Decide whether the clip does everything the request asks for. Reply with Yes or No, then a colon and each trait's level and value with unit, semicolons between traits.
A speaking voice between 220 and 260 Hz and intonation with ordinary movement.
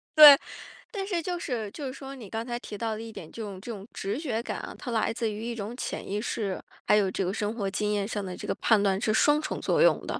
Yes: high, 225 Hz; average, 3.7 semitones